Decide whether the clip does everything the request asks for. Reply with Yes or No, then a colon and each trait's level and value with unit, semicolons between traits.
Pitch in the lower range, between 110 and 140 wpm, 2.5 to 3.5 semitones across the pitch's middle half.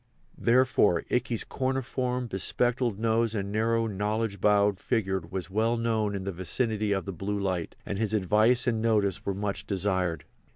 No: low, 105 Hz; average, 165 wpm; average, 2.9 semitones